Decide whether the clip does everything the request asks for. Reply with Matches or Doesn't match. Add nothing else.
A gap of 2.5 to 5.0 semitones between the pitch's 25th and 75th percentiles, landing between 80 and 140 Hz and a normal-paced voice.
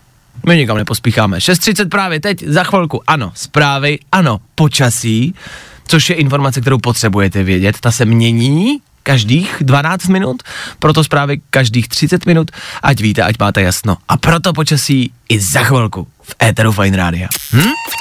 Doesn't match